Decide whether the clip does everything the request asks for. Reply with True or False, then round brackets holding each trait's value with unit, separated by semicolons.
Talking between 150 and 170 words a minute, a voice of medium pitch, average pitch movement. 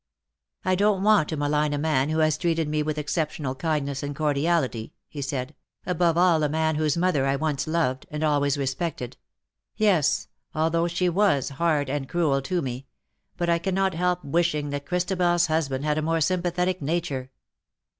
False (190 wpm; 155 Hz; 3.4 semitones)